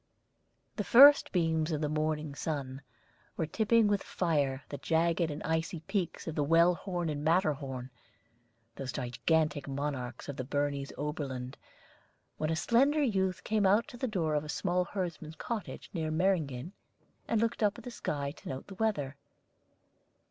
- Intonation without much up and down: No, average, 4.9 semitones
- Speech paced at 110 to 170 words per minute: Yes, average, 165 wpm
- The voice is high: No, medium, 160 Hz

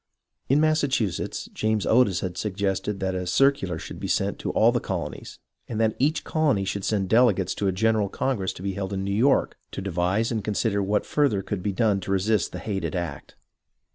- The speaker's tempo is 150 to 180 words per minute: No, average, 200 wpm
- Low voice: Yes, low, 100 Hz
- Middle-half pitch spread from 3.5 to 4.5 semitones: No, average, 2.9 semitones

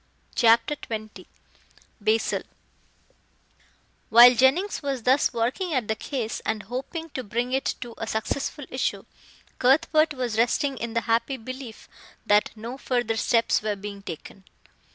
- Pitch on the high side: Yes, high, 240 Hz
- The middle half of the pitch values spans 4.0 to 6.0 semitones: No, average, 3.3 semitones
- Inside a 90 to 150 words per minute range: Yes, slow, 135 wpm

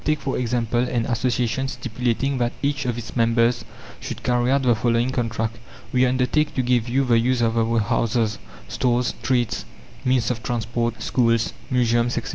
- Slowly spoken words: No, average, 170 wpm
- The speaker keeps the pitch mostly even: Yes, narrow, 1.6 semitones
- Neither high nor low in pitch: No, low, 120 Hz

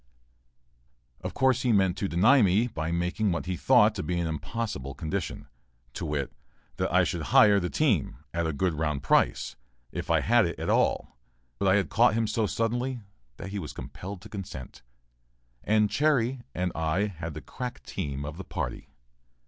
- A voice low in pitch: Yes, very low, 95 Hz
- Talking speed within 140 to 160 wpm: No, average, 185 wpm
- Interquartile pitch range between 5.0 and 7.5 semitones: Yes, wide, 5.4 semitones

